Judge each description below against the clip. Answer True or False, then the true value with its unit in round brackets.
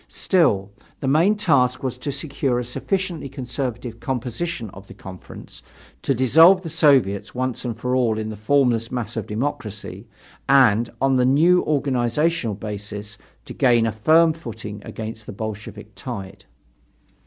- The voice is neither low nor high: False (125 Hz)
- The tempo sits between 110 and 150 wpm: True (145 wpm)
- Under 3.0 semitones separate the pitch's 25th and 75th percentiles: False (4.5 semitones)